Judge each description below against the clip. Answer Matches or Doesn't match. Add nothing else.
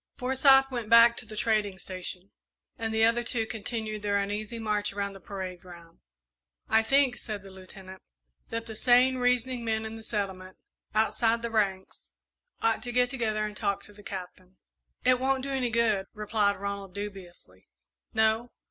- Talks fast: Doesn't match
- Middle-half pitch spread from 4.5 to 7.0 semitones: Doesn't match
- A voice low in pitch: Doesn't match